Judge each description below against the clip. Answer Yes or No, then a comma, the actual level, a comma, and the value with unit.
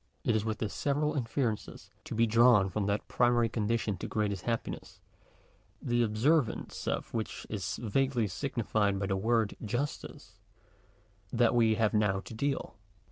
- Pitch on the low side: Yes, low, 115 Hz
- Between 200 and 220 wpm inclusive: No, average, 155 wpm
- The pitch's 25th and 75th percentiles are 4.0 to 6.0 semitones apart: No, narrow, 2.4 semitones